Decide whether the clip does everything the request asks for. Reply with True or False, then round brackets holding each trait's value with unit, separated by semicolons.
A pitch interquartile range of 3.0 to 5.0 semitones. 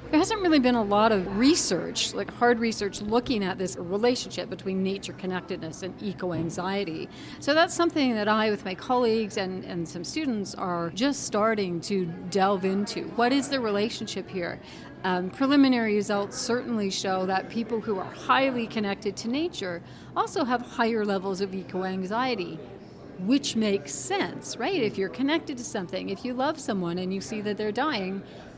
True (4.6 semitones)